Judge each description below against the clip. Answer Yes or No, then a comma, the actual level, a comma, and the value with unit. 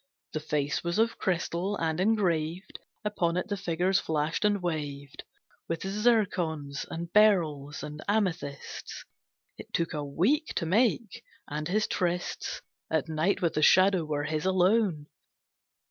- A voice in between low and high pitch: Yes, medium, 170 Hz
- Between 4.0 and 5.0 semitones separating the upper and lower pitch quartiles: Yes, average, 4.5 semitones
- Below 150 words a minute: Yes, average, 140 wpm